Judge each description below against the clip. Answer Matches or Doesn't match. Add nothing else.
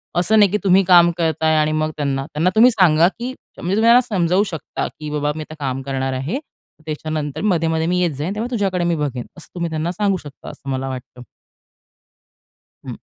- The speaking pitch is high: Doesn't match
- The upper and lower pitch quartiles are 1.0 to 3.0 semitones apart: Doesn't match